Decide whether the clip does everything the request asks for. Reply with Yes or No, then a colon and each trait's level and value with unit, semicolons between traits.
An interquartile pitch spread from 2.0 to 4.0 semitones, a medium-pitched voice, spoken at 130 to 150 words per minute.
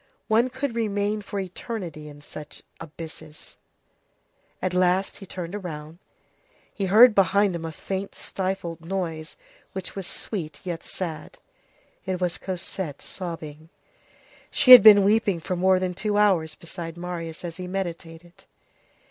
Yes: average, 3.3 semitones; medium, 180 Hz; average, 140 wpm